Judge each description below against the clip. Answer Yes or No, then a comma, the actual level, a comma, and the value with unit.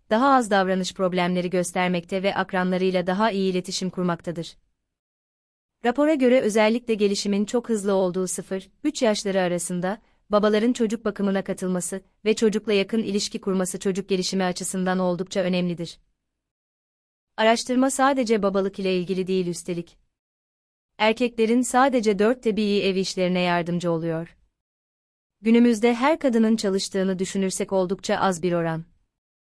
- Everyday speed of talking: Yes, average, 120 wpm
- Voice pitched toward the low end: No, high, 195 Hz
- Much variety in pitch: No, average, 3.3 semitones